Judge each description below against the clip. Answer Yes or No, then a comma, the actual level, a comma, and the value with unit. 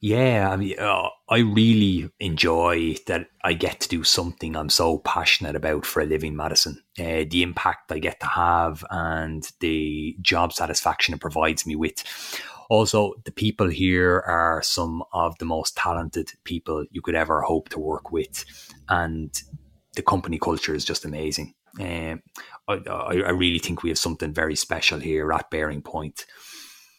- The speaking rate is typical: Yes, average, 165 wpm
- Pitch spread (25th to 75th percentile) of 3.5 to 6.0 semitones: No, narrow, 2.4 semitones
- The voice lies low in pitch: Yes, very low, 85 Hz